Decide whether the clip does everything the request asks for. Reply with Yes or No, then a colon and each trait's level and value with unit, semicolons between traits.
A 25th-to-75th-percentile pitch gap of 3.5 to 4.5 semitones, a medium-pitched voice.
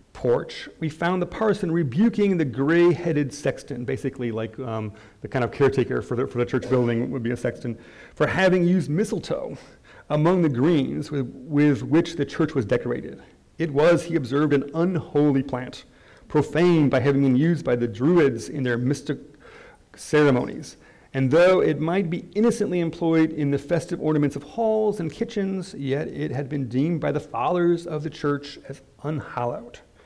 Yes: average, 4.2 semitones; medium, 150 Hz